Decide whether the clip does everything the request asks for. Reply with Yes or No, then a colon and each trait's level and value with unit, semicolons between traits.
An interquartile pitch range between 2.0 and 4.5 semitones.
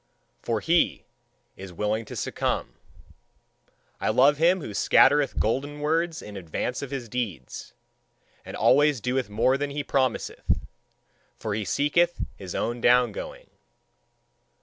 No: average, 5.2 semitones